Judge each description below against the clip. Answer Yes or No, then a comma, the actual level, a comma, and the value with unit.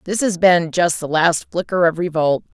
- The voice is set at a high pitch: No, medium, 170 Hz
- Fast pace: Yes, fast, 210 wpm